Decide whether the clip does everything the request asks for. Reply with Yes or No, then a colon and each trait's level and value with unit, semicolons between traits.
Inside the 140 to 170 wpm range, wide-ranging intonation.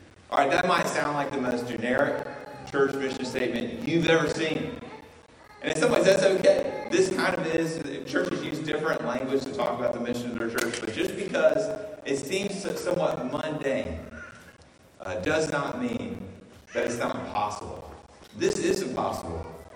Yes: average, 165 wpm; wide, 7.1 semitones